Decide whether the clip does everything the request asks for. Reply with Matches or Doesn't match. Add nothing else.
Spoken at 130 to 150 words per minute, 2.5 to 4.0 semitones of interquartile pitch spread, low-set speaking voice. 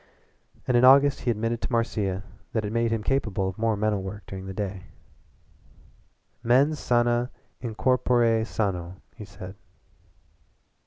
Matches